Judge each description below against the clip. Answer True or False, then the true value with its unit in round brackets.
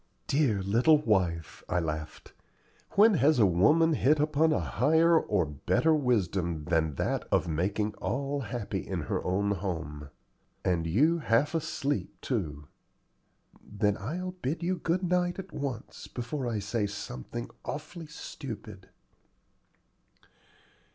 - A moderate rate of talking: False (125 wpm)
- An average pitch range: False (8.8 semitones)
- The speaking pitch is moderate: False (115 Hz)